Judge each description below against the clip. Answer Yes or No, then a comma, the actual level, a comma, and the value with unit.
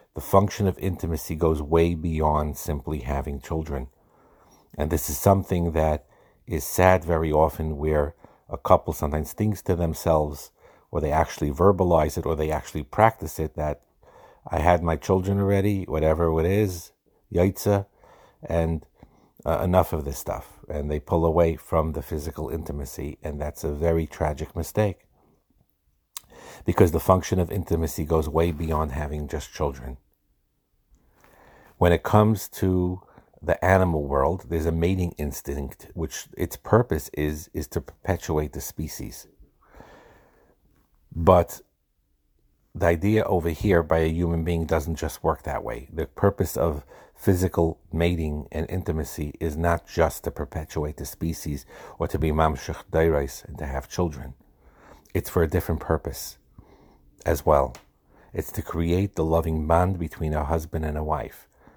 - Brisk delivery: No, average, 150 wpm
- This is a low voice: Yes, very low, 80 Hz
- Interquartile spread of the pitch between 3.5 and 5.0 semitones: No, average, 2.8 semitones